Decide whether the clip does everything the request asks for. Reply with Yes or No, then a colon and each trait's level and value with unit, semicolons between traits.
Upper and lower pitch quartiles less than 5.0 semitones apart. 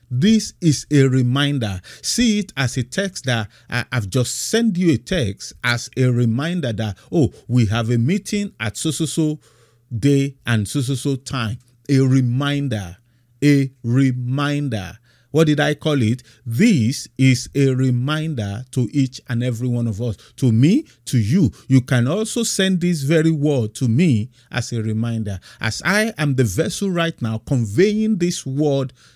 Yes: average, 4.2 semitones